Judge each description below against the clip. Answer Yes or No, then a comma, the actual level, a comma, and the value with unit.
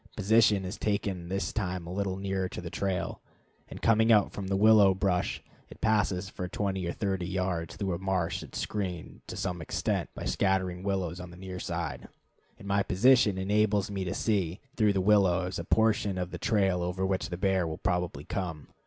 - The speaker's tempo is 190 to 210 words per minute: Yes, average, 195 wpm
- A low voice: Yes, very low, 95 Hz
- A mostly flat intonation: Yes, narrow, 2.1 semitones